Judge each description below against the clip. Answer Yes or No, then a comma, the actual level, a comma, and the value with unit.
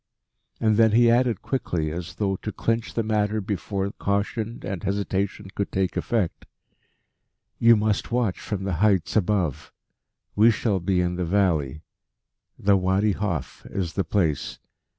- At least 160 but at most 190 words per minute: No, average, 150 wpm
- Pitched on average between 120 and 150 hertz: No, low, 100 Hz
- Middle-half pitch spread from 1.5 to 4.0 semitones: Yes, average, 3.2 semitones